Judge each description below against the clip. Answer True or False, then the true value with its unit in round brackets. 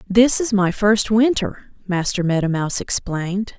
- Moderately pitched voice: False (200 Hz)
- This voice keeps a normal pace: True (150 wpm)